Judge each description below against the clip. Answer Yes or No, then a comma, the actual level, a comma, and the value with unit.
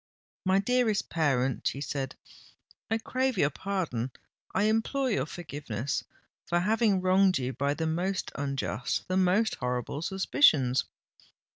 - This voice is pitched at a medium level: Yes, medium, 175 Hz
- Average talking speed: No, slow, 120 wpm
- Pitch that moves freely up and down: Yes, wide, 6.5 semitones